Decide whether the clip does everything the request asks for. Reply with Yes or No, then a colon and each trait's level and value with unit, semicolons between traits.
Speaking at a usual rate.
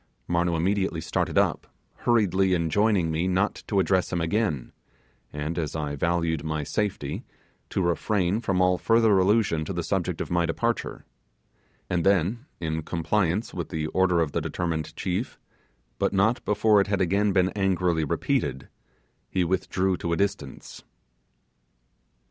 Yes: average, 150 wpm